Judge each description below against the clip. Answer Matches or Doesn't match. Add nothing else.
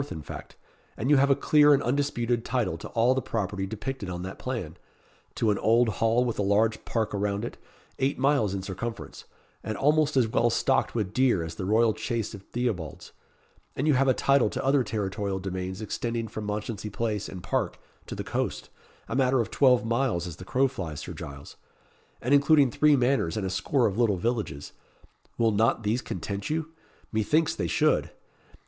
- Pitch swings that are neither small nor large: Matches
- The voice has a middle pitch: Doesn't match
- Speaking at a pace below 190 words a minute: Doesn't match